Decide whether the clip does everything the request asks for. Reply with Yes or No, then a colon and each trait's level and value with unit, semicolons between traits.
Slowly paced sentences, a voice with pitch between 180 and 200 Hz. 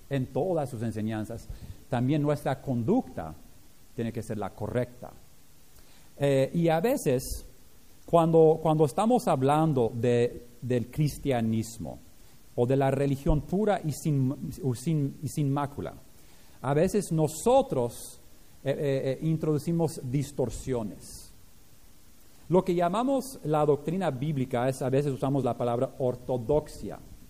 No: slow, 120 wpm; low, 135 Hz